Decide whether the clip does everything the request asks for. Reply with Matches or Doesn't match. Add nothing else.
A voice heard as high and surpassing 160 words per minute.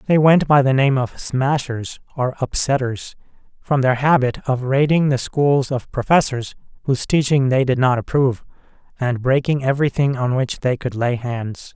Doesn't match